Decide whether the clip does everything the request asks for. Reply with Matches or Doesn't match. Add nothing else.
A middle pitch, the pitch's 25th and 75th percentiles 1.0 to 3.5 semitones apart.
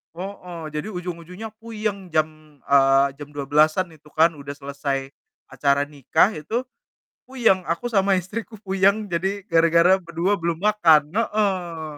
Doesn't match